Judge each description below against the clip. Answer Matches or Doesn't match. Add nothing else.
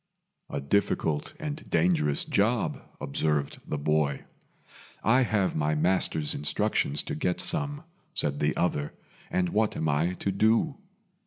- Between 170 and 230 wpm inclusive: Doesn't match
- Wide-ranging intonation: Matches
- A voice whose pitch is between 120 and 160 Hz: Doesn't match